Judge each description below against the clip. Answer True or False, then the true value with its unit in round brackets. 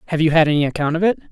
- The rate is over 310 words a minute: True (320 wpm)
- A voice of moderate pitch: True (155 Hz)